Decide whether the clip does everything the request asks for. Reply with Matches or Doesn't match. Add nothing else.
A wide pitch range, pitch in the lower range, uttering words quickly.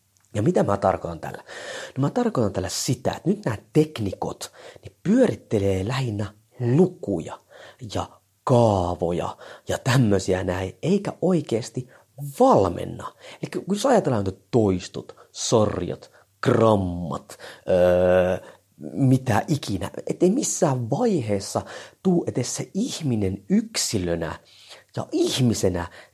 Doesn't match